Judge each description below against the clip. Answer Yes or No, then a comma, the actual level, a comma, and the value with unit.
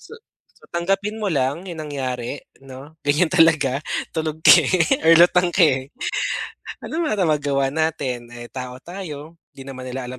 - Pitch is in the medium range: Yes, medium, 150 Hz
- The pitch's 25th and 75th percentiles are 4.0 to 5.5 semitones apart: Yes, average, 4.4 semitones